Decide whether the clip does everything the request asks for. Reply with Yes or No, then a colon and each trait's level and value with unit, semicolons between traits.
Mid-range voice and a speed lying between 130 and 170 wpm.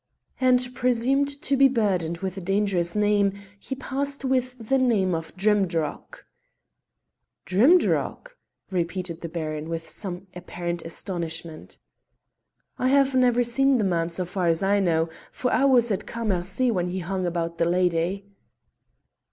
No: high, 195 Hz; average, 145 wpm